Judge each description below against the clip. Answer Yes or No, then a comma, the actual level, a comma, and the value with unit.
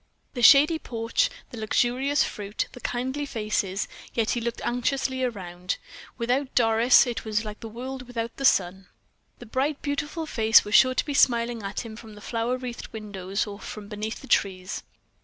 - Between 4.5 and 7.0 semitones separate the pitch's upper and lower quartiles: No, average, 3.3 semitones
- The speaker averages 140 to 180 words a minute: Yes, average, 175 wpm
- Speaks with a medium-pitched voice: No, high, 235 Hz